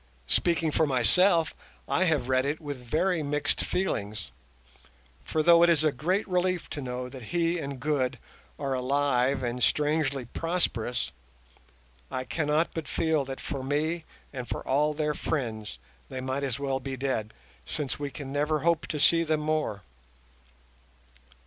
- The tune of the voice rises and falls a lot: No, average, 3.6 semitones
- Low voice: No, medium, 145 Hz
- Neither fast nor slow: Yes, average, 155 wpm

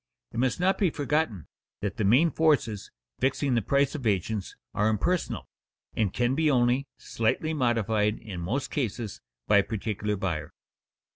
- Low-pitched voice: Yes, low, 115 Hz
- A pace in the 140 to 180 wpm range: Yes, average, 155 wpm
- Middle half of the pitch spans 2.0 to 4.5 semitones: No, average, 5.1 semitones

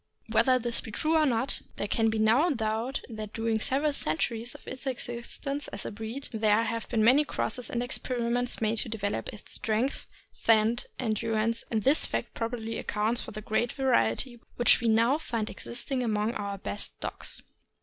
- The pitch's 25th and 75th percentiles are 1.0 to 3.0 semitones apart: Yes, narrow, 2.4 semitones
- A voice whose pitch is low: No, high, 230 Hz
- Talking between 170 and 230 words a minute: Yes, average, 185 wpm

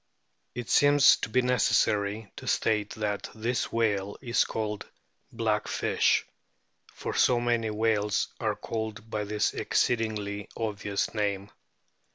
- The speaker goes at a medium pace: No, slow, 125 wpm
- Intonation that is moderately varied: No, narrow, 1.9 semitones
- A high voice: No, low, 110 Hz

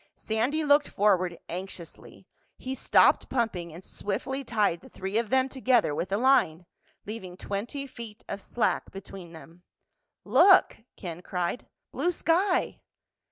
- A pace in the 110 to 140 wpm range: Yes, slow, 135 wpm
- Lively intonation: Yes, wide, 6.5 semitones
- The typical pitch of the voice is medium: No, high, 210 Hz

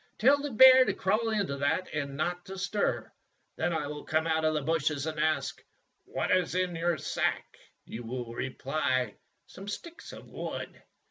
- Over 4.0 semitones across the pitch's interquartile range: Yes, average, 5.2 semitones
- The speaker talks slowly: No, average, 180 wpm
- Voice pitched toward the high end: No, medium, 160 Hz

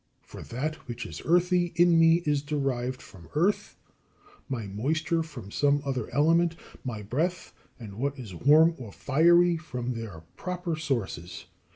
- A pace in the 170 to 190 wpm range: No, average, 150 wpm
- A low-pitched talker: No, medium, 145 Hz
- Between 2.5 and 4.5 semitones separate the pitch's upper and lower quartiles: No, wide, 5.4 semitones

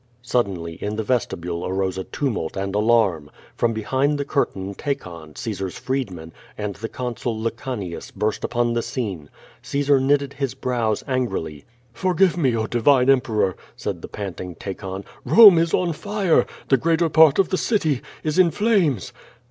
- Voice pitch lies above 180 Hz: No, low, 120 Hz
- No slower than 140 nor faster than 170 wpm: Yes, average, 160 wpm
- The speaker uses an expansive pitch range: Yes, wide, 6.6 semitones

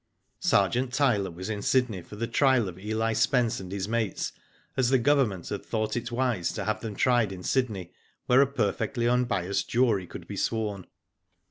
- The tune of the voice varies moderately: Yes, average, 3.8 semitones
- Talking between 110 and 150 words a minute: No, average, 180 wpm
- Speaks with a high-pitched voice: No, low, 115 Hz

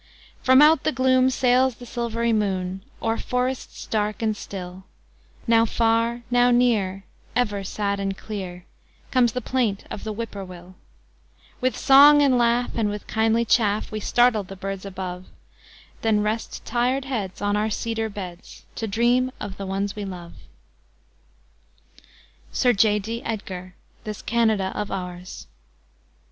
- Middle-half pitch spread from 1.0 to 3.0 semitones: No, average, 3.6 semitones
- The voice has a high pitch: Yes, high, 220 Hz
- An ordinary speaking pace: Yes, average, 150 wpm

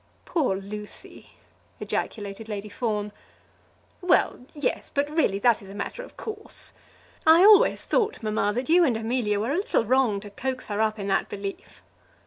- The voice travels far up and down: Yes, wide, 5.9 semitones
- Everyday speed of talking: Yes, average, 165 wpm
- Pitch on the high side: Yes, high, 225 Hz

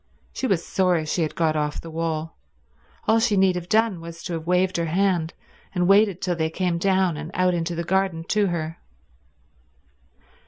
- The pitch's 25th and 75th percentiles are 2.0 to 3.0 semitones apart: Yes, narrow, 2.6 semitones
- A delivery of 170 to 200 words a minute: Yes, average, 190 wpm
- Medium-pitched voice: Yes, medium, 175 Hz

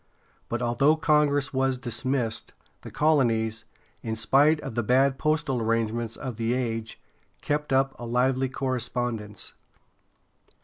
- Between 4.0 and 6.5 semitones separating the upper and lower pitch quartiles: No, average, 3.1 semitones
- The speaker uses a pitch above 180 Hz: No, low, 125 Hz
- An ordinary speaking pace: No, slow, 125 wpm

